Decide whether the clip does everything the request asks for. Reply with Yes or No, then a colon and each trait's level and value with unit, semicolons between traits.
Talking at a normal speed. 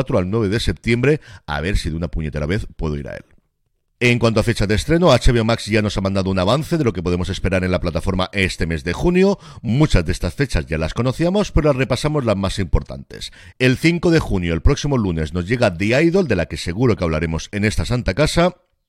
No: fast, 240 wpm